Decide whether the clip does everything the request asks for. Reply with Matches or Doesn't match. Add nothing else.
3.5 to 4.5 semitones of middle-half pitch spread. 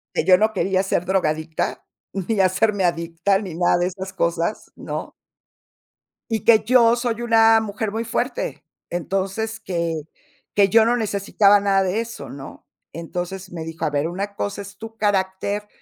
Matches